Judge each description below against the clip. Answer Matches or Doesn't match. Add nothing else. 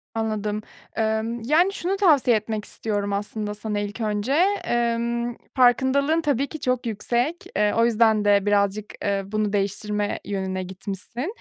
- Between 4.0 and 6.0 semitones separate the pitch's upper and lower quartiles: Doesn't match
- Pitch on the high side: Matches